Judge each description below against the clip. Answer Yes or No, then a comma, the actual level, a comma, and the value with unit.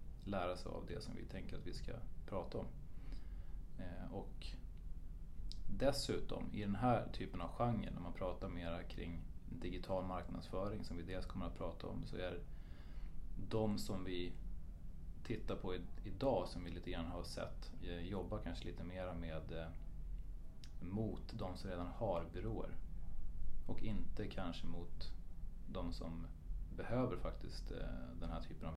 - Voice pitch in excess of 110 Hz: No, very low, 85 Hz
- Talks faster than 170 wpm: No, average, 150 wpm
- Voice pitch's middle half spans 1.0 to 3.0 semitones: Yes, narrow, 2.5 semitones